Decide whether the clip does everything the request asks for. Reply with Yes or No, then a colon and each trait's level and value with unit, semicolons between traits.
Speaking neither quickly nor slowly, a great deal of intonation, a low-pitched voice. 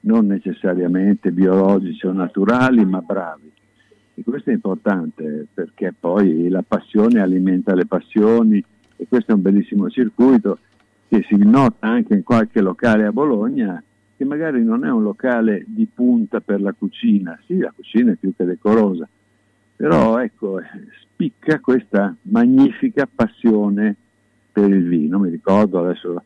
Yes: average, 145 wpm; wide, 6.2 semitones; low, 105 Hz